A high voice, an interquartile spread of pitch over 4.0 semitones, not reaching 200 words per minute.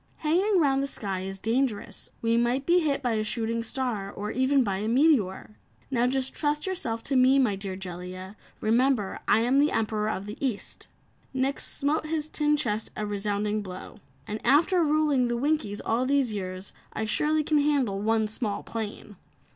Yes: high, 235 Hz; average, 5.1 semitones; average, 180 wpm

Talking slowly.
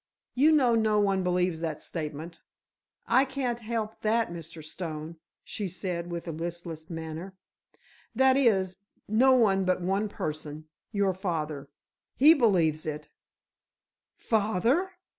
Yes: slow, 125 wpm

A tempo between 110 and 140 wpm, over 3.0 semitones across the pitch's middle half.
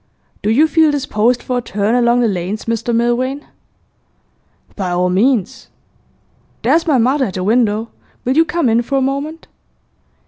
No: average, 165 wpm; average, 4.1 semitones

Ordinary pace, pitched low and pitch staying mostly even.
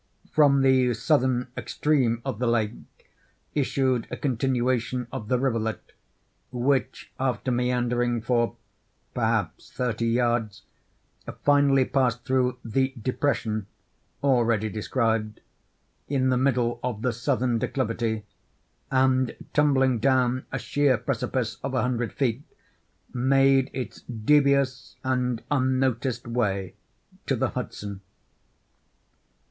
No: slow, 110 wpm; low, 125 Hz; narrow, 2.2 semitones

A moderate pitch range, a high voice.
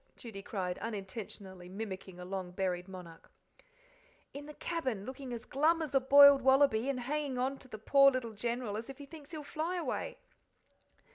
No: wide, 6.2 semitones; high, 245 Hz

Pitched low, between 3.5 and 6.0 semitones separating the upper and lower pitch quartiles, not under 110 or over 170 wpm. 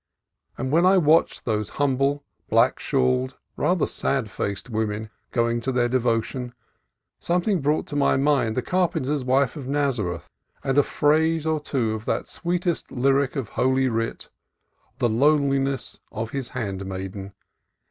Yes: low, 130 Hz; average, 4.4 semitones; average, 150 wpm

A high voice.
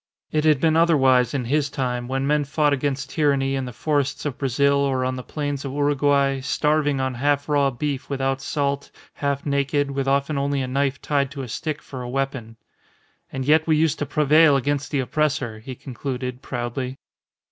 No: medium, 140 Hz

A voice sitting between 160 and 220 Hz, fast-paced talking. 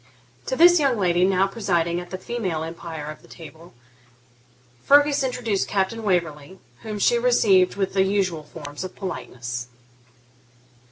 No: high, 190 Hz; average, 150 wpm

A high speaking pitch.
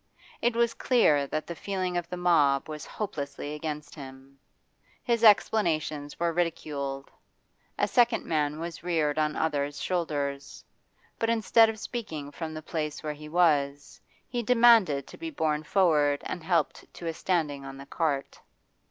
No: medium, 155 Hz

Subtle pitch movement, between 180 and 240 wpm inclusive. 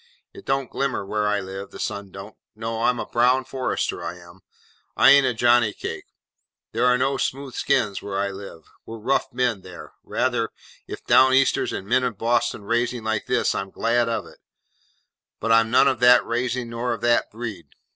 No: average, 3.4 semitones; average, 195 wpm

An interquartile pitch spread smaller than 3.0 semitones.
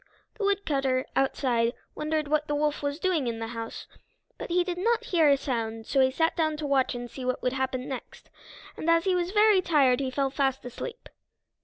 No: average, 4.6 semitones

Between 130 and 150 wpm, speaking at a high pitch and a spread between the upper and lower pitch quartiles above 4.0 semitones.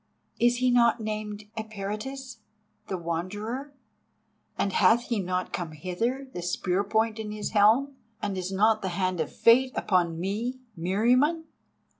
Yes: average, 145 wpm; high, 215 Hz; average, 4.4 semitones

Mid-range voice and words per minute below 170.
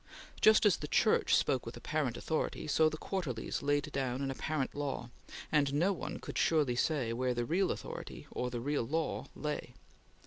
No: medium, 145 Hz; average, 180 wpm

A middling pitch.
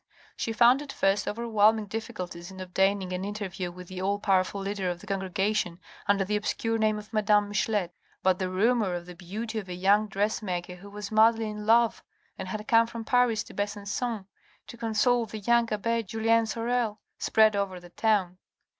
No: high, 210 Hz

